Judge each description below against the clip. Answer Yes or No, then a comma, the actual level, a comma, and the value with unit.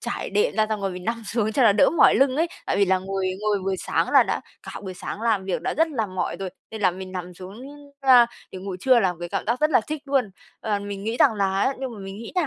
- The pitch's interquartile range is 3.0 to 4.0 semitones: No, average, 4.5 semitones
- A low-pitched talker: No, high, 210 Hz